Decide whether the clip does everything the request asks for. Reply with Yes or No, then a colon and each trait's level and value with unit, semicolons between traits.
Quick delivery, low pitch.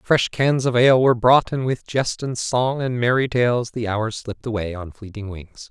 Yes: fast, 220 wpm; low, 120 Hz